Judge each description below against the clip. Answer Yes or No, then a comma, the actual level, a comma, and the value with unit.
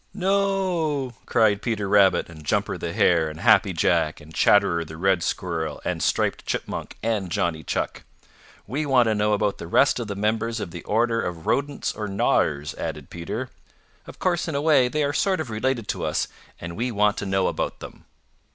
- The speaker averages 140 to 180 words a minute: No, average, 195 wpm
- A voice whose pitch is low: Yes, low, 105 Hz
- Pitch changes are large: Yes, wide, 7.2 semitones